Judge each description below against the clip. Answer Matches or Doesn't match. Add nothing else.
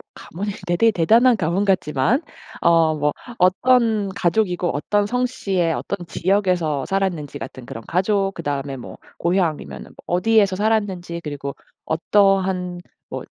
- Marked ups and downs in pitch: Doesn't match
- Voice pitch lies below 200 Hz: Matches